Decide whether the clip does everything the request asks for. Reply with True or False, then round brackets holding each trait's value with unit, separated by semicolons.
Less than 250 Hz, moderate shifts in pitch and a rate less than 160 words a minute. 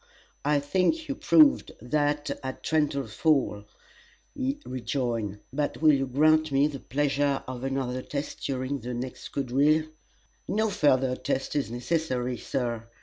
True (140 Hz; 3.1 semitones; 140 wpm)